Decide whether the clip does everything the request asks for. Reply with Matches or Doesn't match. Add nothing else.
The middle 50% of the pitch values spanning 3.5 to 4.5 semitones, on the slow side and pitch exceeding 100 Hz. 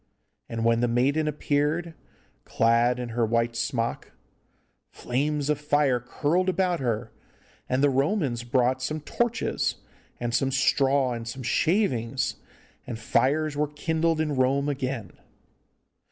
Matches